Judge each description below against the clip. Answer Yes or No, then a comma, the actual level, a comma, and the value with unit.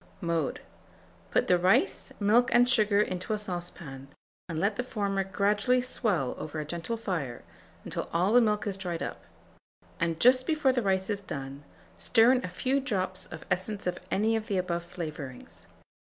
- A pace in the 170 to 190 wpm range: Yes, average, 175 wpm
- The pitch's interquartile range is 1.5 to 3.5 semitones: No, average, 4.5 semitones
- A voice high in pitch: Yes, high, 195 Hz